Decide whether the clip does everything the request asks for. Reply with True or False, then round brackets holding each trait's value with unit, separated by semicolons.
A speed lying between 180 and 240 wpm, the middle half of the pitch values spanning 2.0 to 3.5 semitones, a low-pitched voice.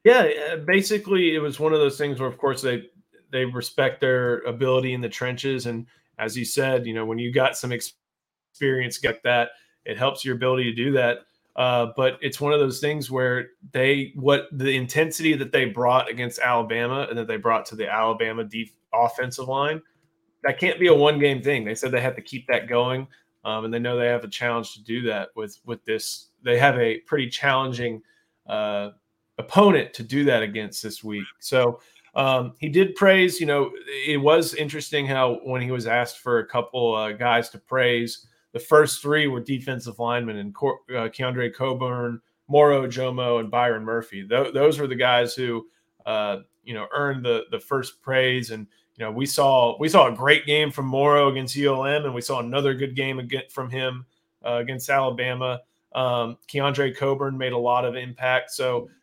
True (195 wpm; 2.8 semitones; 130 Hz)